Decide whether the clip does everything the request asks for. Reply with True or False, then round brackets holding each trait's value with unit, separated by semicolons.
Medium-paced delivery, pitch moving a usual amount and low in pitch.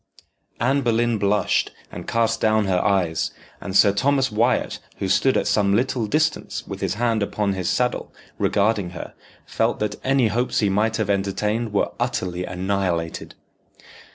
True (155 wpm; 3.2 semitones; 105 Hz)